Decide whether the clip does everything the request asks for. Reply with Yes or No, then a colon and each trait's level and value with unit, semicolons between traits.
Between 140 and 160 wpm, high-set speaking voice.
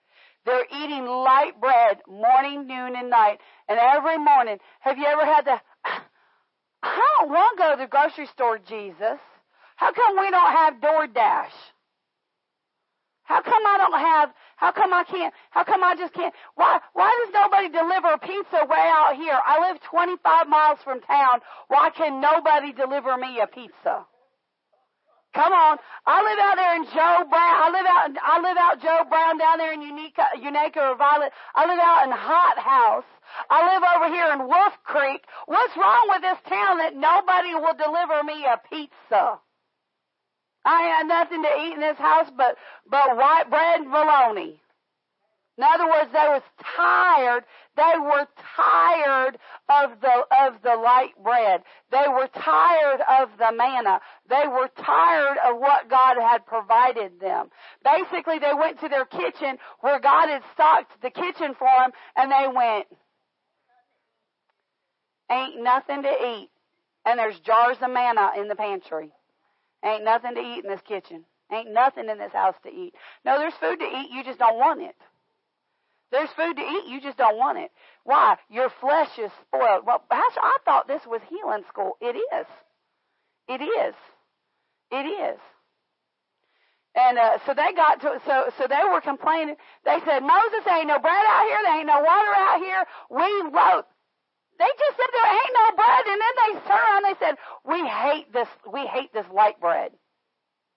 No: average, 175 wpm; very high, 295 Hz